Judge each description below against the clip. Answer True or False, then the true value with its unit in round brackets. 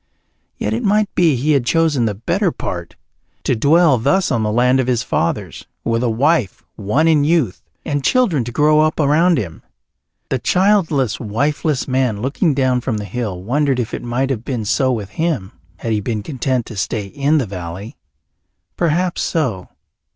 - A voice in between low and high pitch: False (130 Hz)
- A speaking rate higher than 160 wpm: True (180 wpm)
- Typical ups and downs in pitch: False (5.7 semitones)